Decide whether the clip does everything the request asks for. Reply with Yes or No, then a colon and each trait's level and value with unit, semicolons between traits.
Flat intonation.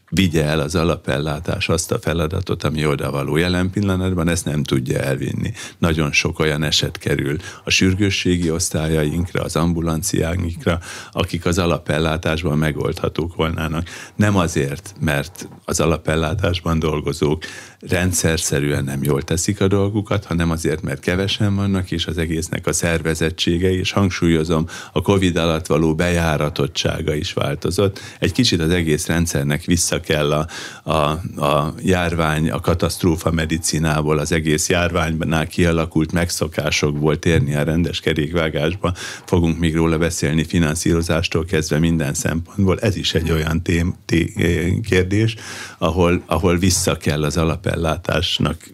Yes: narrow, 2.3 semitones